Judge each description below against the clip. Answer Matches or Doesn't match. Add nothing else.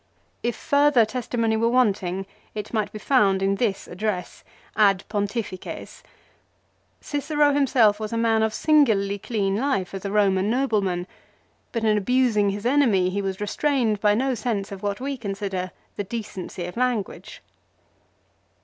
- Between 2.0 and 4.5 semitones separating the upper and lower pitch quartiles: Matches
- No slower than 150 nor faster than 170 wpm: Matches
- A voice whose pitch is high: Matches